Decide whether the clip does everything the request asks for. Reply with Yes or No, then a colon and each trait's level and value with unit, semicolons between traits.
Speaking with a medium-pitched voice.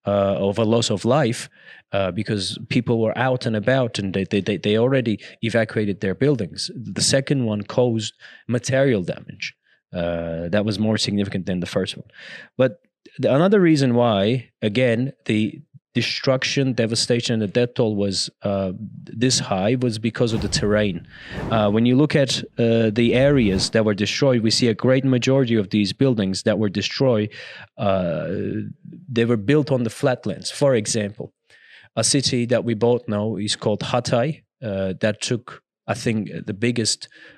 No: low, 115 Hz